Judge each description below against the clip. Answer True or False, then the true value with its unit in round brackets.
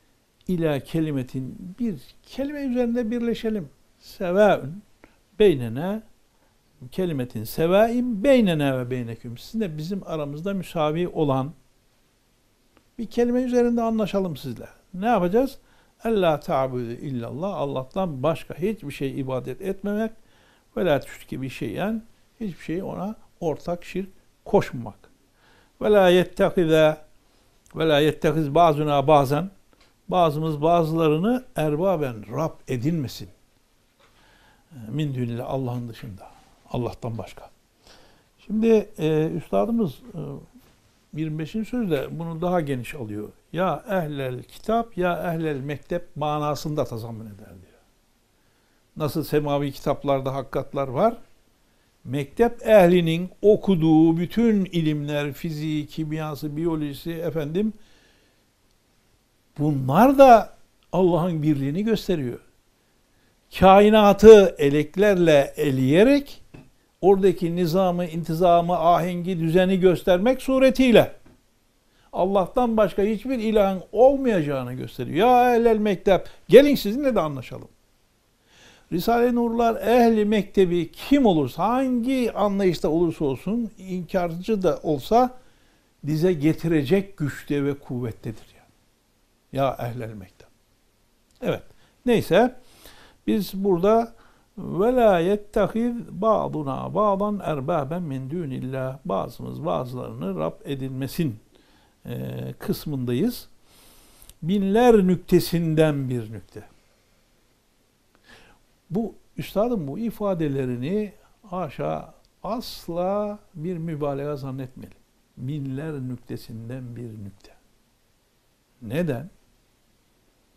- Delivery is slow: True (90 wpm)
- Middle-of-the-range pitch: True (165 Hz)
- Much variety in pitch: True (7.1 semitones)